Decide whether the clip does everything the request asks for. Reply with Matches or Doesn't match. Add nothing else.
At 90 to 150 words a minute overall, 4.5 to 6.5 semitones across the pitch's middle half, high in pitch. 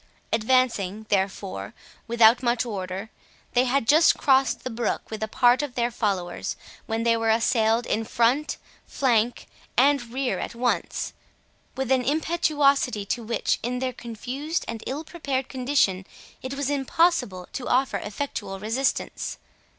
Doesn't match